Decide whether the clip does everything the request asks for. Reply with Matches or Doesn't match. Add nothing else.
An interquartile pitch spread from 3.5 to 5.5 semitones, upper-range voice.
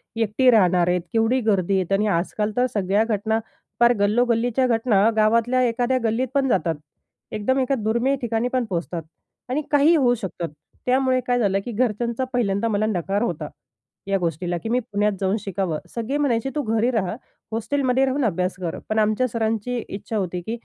Matches